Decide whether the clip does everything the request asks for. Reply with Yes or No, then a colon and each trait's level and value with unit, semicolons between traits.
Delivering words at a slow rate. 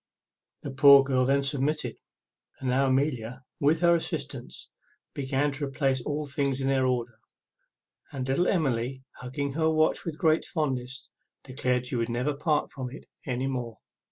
No: average, 155 wpm